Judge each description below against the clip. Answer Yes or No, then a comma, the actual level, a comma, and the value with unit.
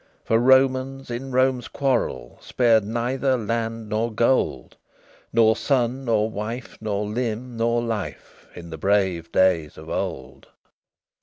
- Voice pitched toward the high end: No, low, 115 Hz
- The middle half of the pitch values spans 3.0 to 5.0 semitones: Yes, average, 3.4 semitones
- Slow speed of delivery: Yes, slow, 130 wpm